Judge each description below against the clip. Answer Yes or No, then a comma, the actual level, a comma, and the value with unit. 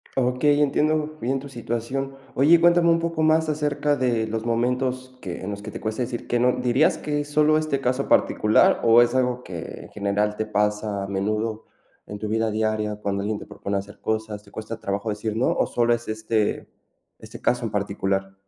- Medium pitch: No, low, 115 Hz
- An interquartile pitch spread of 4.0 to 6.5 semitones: Yes, average, 4.4 semitones